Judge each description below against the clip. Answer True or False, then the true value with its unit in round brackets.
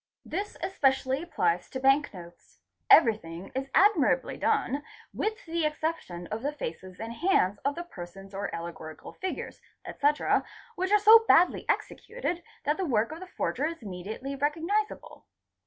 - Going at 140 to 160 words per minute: True (150 wpm)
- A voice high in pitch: True (280 Hz)